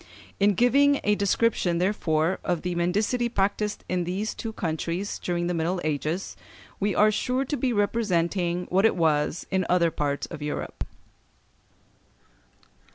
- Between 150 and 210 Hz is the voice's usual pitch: Yes, medium, 185 Hz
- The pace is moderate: Yes, average, 145 wpm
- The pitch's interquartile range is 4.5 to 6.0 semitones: No, average, 3.7 semitones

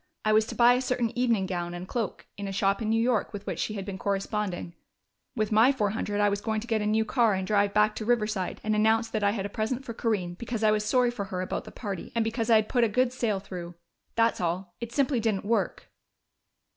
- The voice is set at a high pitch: Yes, high, 215 Hz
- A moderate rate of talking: No, fast, 260 wpm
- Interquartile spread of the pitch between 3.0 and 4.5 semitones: No, narrow, 2.6 semitones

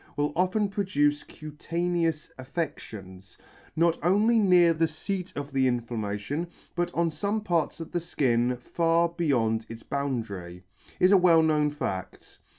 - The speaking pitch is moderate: Yes, medium, 155 Hz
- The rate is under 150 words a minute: Yes, average, 140 wpm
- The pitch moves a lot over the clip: Yes, wide, 5.7 semitones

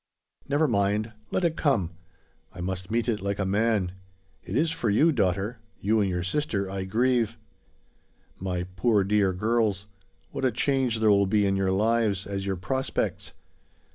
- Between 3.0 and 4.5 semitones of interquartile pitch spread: Yes, average, 3.4 semitones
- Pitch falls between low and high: No, low, 105 Hz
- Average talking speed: Yes, average, 170 wpm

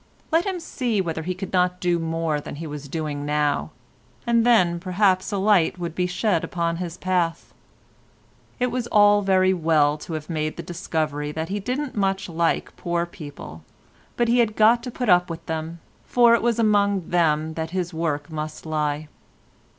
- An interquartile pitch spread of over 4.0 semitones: Yes, average, 4.4 semitones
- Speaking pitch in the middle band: Yes, medium, 175 Hz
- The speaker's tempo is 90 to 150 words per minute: No, average, 190 wpm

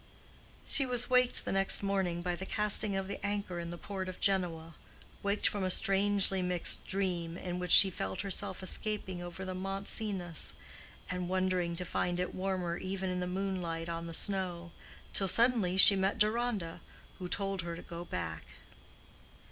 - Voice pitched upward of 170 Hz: Yes, medium, 185 Hz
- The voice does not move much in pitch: Yes, narrow, 2.1 semitones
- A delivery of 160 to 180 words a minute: Yes, average, 170 wpm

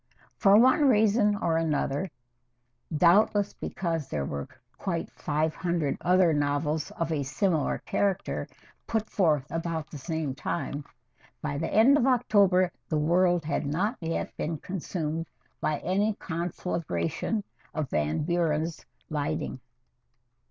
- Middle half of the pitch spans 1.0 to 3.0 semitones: No, average, 4.4 semitones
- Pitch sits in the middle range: Yes, medium, 165 Hz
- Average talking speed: No, slow, 125 wpm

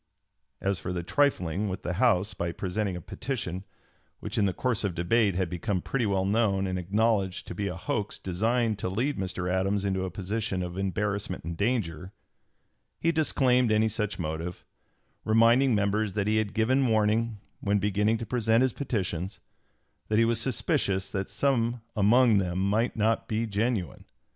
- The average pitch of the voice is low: Yes, low, 105 Hz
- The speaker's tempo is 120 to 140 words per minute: No, average, 170 wpm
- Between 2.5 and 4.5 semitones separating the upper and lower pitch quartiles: Yes, average, 3.5 semitones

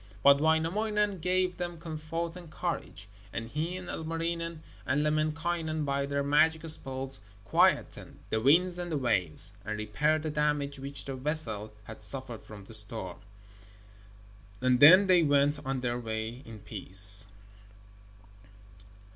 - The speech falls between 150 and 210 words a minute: No, average, 140 wpm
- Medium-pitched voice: Yes, medium, 145 Hz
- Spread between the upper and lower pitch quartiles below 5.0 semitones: No, wide, 5.4 semitones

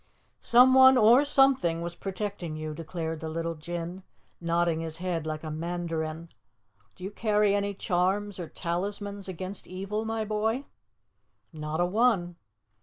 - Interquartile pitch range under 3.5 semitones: No, average, 3.9 semitones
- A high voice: No, medium, 180 Hz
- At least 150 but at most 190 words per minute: No, average, 140 wpm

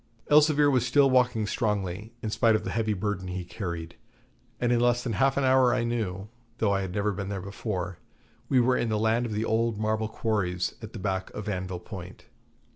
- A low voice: Yes, low, 110 Hz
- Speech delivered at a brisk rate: Yes, fast, 210 wpm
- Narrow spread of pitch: No, average, 3.8 semitones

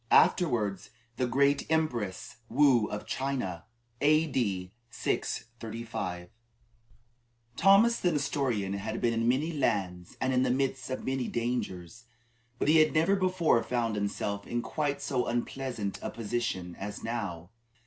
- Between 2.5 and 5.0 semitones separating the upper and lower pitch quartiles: No, wide, 5.4 semitones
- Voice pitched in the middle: No, low, 120 Hz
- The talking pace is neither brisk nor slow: No, slow, 130 wpm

